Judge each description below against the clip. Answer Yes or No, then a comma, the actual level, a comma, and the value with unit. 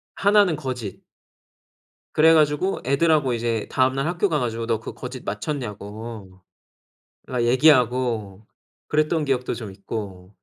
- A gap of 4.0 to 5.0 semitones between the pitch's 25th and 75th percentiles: No, wide, 5.5 semitones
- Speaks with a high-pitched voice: No, low, 125 Hz